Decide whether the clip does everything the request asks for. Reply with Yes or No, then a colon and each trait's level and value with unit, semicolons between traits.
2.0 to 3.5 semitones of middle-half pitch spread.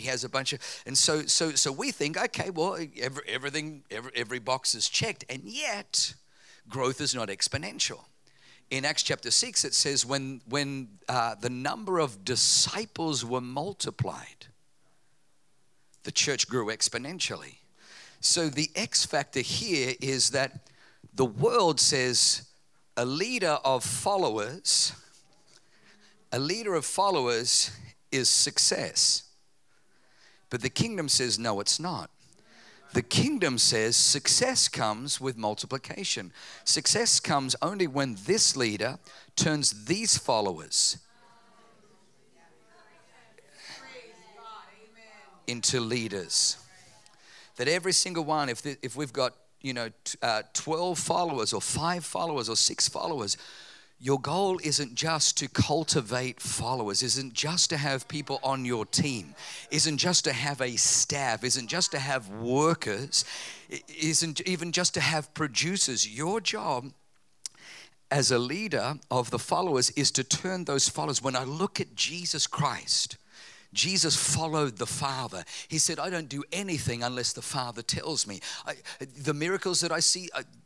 No: average, 4.4 semitones